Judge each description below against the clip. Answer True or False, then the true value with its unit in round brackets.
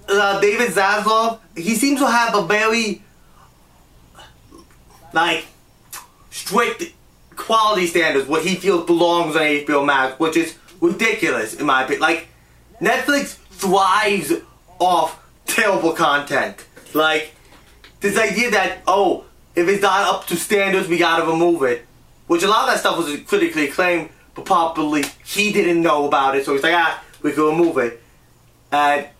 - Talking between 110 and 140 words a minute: False (150 wpm)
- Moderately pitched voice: True (175 Hz)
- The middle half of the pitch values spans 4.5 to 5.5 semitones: True (5.0 semitones)